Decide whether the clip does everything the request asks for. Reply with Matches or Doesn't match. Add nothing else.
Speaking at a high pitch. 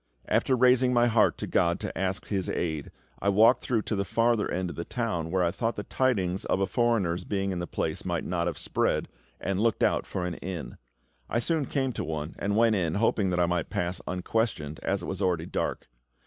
Doesn't match